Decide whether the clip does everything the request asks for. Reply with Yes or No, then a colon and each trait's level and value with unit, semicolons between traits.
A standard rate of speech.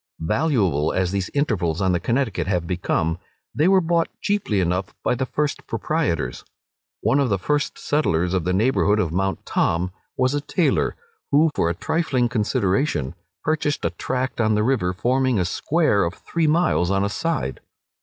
Yes: average, 175 wpm